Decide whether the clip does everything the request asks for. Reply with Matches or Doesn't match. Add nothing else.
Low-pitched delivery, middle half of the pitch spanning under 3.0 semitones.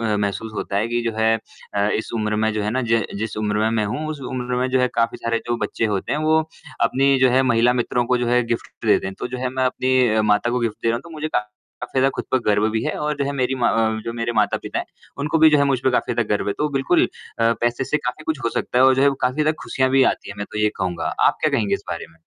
Doesn't match